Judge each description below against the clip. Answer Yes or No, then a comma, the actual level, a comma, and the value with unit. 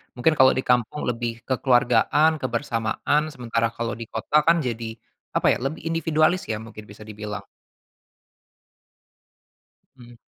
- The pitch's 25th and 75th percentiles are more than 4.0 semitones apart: Yes, average, 4.5 semitones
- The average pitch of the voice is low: Yes, low, 120 Hz